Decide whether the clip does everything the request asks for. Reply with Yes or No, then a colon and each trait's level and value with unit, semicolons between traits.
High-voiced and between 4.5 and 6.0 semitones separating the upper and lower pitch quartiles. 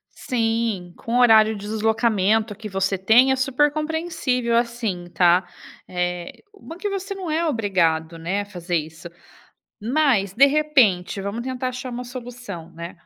Yes: high, 225 Hz; wide, 5.5 semitones